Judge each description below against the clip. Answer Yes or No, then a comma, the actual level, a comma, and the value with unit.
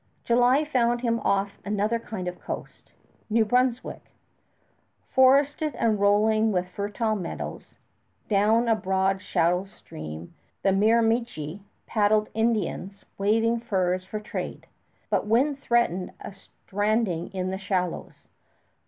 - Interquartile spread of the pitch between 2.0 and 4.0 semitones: Yes, average, 3.4 semitones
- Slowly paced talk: Yes, slow, 120 wpm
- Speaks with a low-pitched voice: No, high, 210 Hz